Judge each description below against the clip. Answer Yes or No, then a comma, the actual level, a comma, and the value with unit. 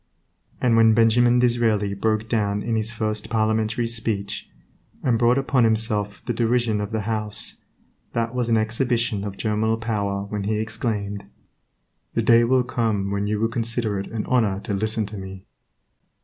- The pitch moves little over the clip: Yes, narrow, 2.0 semitones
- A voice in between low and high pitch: No, low, 110 Hz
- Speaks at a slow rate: No, average, 165 wpm